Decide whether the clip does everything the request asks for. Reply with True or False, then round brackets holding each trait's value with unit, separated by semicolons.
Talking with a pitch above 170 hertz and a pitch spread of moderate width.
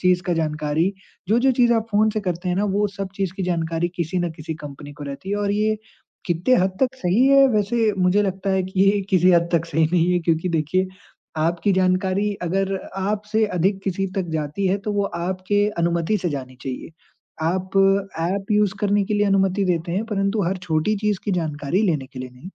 True (185 Hz; 3.3 semitones)